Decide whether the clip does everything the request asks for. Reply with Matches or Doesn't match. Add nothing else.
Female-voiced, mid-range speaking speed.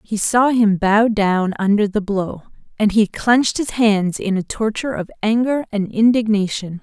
Matches